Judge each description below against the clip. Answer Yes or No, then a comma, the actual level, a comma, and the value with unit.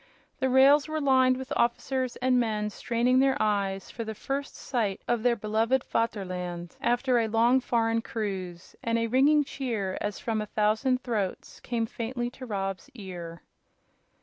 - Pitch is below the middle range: No, high, 230 Hz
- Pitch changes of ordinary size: Yes, average, 3.6 semitones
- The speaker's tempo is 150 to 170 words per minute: Yes, average, 160 wpm